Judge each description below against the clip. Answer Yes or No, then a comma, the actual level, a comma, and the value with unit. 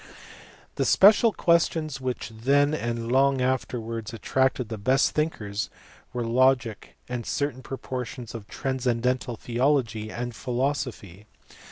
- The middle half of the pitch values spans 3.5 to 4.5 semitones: No, average, 2.7 semitones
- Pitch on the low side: Yes, low, 125 Hz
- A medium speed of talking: No, slow, 115 wpm